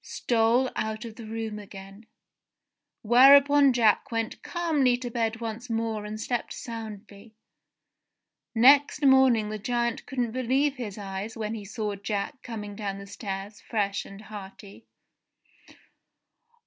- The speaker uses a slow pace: Yes, slow, 130 wpm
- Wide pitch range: No, average, 2.8 semitones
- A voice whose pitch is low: No, high, 225 Hz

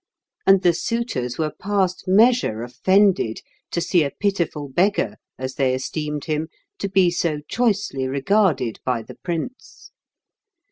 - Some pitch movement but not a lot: No, wide, 6.8 semitones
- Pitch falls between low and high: Yes, medium, 170 Hz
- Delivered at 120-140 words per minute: Yes, slow, 135 wpm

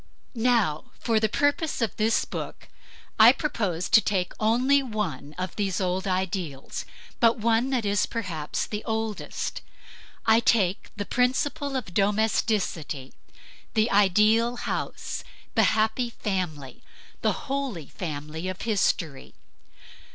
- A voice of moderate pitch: No, high, 210 Hz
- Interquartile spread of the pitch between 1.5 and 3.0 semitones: No, average, 4.2 semitones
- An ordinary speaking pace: No, slow, 120 wpm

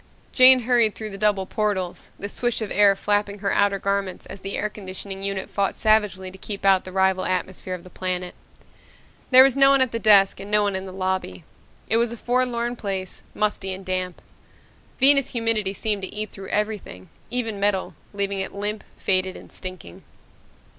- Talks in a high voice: Yes, high, 200 Hz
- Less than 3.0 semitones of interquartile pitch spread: Yes, narrow, 2.4 semitones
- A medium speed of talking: Yes, average, 190 wpm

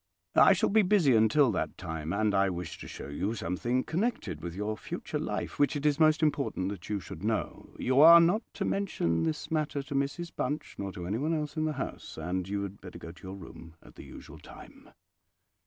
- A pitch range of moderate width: No, wide, 8.8 semitones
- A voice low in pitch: Yes, low, 110 Hz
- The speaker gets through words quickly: Yes, fast, 220 wpm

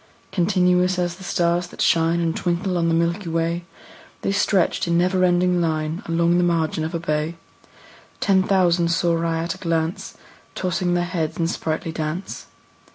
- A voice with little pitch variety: Yes, narrow, 1.4 semitones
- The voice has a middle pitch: Yes, medium, 170 Hz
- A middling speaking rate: Yes, average, 170 wpm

